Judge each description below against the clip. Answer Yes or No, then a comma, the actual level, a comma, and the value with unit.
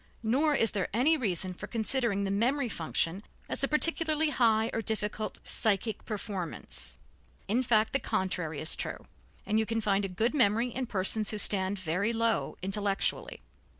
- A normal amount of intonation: Yes, average, 3.5 semitones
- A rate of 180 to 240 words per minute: No, average, 165 wpm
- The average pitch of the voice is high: Yes, high, 220 Hz